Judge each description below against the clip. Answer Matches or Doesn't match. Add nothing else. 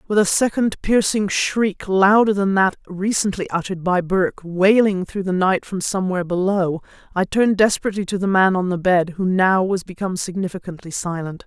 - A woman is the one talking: Matches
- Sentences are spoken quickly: Doesn't match